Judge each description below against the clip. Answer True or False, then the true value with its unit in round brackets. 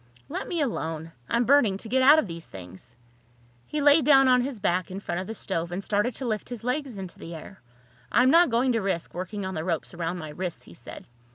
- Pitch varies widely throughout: True (6.7 semitones)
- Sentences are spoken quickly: True (240 wpm)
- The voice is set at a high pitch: True (205 Hz)